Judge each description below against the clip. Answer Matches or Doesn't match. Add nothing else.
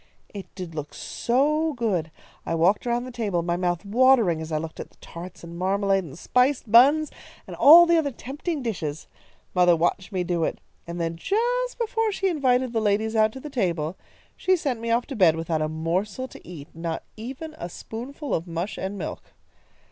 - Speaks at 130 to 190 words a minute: Doesn't match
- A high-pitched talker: Matches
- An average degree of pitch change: Doesn't match